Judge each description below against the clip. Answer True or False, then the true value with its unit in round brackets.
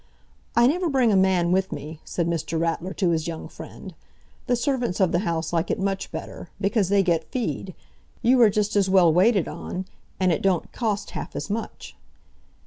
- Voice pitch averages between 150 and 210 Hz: True (190 Hz)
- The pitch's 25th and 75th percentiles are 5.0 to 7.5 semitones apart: False (4.2 semitones)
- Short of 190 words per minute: False (195 wpm)